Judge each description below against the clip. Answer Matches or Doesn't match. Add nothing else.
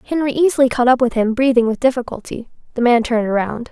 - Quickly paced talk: Matches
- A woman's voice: Matches